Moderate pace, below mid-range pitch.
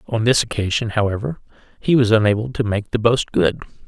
Yes: average, 185 wpm; low, 110 Hz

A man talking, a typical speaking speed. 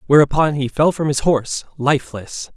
Yes: male; average, 165 wpm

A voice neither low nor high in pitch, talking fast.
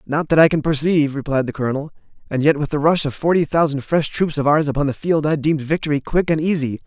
Yes: medium, 150 Hz; fast, 255 wpm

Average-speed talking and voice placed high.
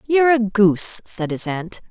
Yes: average, 190 wpm; high, 215 Hz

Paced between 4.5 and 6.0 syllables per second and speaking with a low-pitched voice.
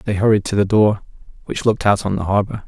No: 6.4 syllables/s; low, 105 Hz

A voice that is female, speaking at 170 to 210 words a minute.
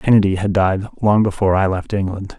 No: male; average, 200 wpm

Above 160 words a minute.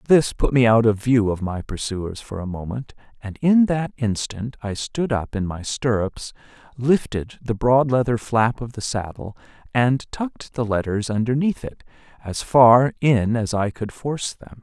Yes: average, 180 wpm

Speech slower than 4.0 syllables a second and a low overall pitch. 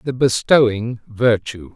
Yes: 3.6 syllables/s; low, 115 Hz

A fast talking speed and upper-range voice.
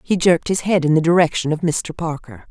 No: fast, 240 wpm; medium, 165 Hz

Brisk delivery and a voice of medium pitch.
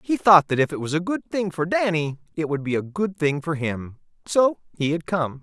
Yes: fast, 255 wpm; medium, 165 Hz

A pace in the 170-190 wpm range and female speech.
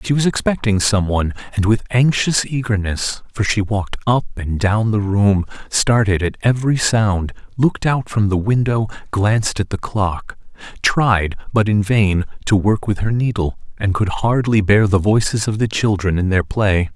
No: average, 180 wpm; male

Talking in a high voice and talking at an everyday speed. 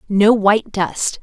Yes: high, 205 Hz; average, 145 wpm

